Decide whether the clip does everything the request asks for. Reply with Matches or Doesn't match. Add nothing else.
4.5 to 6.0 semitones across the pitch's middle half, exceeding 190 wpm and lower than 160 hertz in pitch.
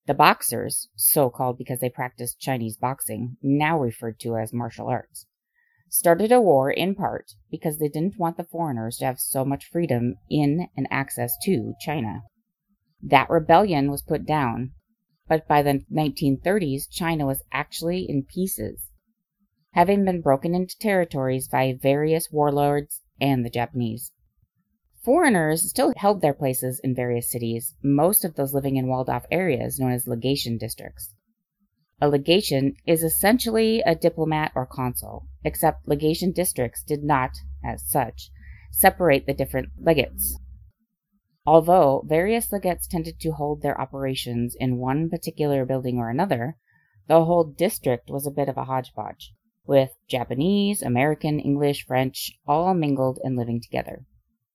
Doesn't match